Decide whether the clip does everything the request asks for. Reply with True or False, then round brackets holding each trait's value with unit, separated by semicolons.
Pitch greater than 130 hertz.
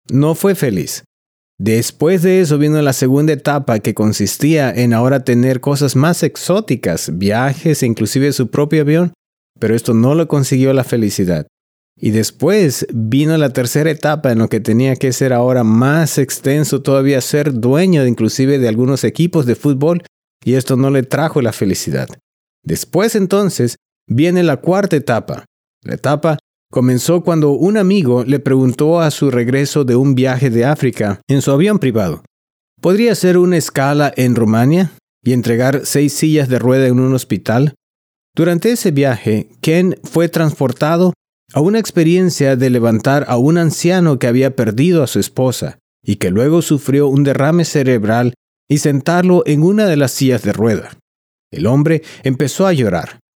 True (140 Hz)